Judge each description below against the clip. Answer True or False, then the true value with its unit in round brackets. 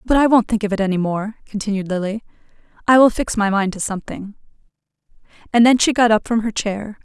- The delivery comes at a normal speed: False (215 wpm)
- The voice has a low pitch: False (215 Hz)